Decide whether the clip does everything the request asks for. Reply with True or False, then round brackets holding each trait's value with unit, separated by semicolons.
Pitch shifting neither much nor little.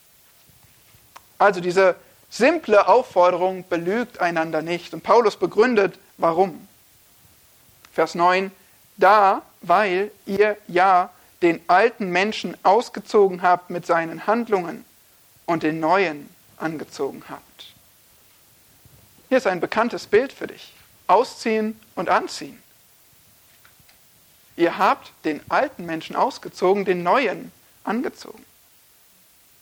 True (3.6 semitones)